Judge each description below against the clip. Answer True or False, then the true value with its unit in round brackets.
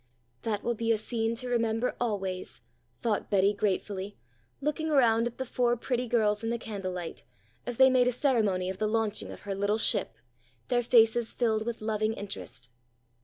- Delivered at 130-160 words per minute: False (175 wpm)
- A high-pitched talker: True (225 Hz)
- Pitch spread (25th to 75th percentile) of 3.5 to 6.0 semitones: False (2.7 semitones)